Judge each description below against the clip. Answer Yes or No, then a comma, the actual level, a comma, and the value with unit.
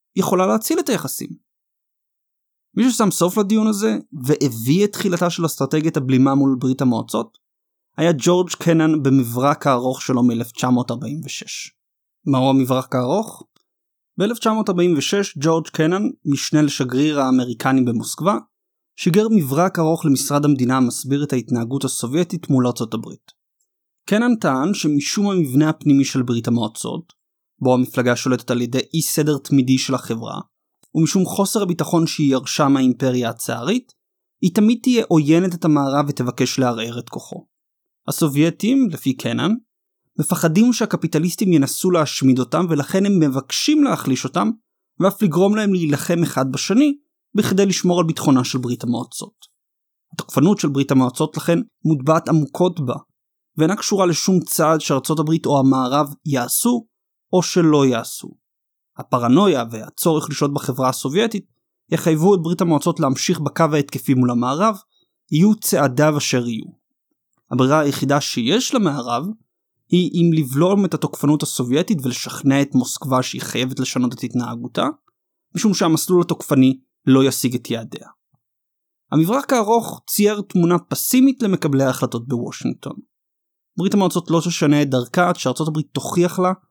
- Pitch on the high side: No, medium, 155 Hz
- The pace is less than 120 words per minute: No, average, 130 wpm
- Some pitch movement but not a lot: No, wide, 5.9 semitones